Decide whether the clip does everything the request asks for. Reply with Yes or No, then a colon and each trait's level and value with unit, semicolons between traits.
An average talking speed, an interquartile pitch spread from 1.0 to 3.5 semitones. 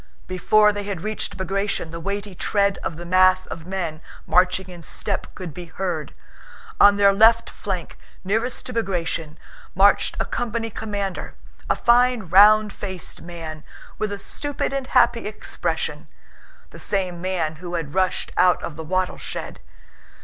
Yes: average, 150 wpm; average, 3.2 semitones